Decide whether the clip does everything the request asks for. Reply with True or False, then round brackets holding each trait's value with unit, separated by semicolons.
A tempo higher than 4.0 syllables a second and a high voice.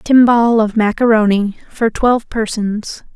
True (4.5 syllables/s; 220 Hz)